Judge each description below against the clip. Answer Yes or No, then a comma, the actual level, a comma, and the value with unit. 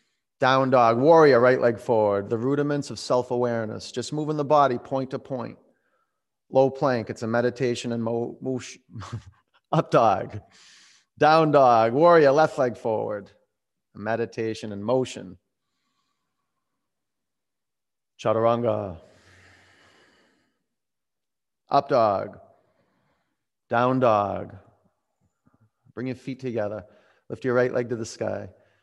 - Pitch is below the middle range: Yes, low, 120 Hz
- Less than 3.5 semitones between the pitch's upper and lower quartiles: Yes, average, 2.9 semitones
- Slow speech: Yes, slow, 110 wpm